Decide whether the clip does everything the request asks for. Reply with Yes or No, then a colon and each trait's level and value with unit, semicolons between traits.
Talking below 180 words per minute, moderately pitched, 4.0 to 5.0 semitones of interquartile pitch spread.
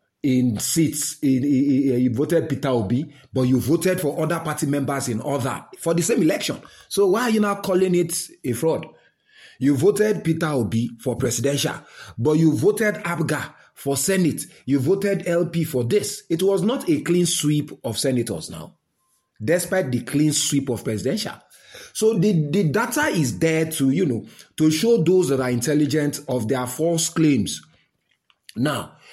Yes: average, 165 wpm; medium, 150 Hz; average, 4.6 semitones